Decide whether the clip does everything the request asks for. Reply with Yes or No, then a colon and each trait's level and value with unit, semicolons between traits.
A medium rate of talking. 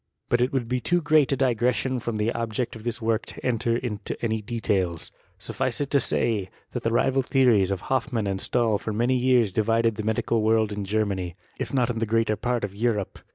No: fast, 215 wpm